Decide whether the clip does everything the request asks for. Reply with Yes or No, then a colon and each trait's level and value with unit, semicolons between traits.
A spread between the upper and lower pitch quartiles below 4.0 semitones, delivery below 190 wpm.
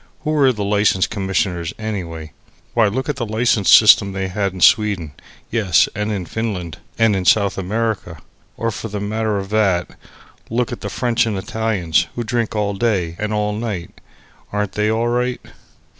Yes: average, 2.8 semitones; average, 175 wpm